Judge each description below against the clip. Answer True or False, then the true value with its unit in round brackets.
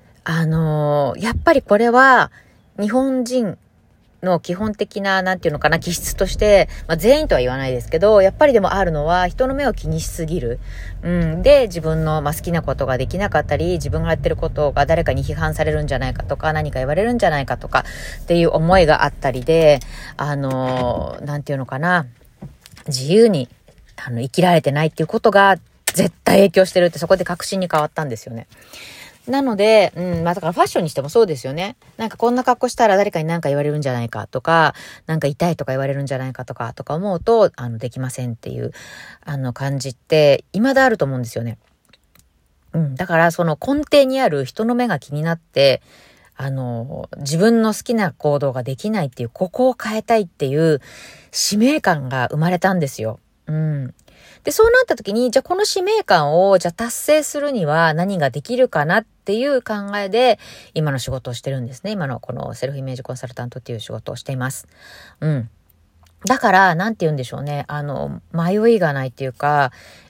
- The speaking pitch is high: False (160 Hz)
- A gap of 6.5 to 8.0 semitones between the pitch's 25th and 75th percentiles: True (7.0 semitones)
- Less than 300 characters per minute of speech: False (405 characters per minute)